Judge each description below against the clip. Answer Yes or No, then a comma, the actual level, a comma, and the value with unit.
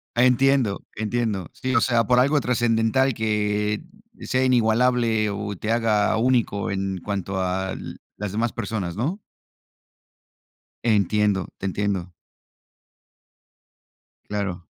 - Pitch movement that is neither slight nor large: Yes, average, 3.1 semitones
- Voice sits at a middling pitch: No, low, 110 Hz